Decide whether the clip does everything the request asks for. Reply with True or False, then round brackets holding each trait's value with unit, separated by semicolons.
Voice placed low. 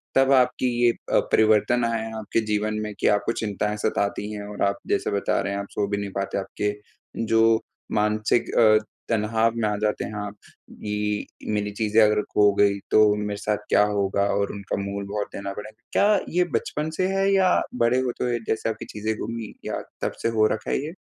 True (105 Hz)